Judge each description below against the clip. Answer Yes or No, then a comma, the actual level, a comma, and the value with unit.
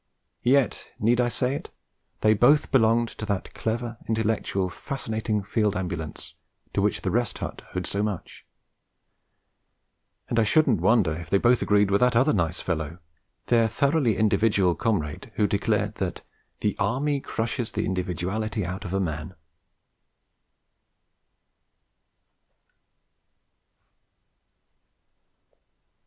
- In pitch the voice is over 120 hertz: No, low, 110 Hz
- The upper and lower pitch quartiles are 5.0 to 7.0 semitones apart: No, average, 3.9 semitones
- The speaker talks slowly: Yes, slow, 120 wpm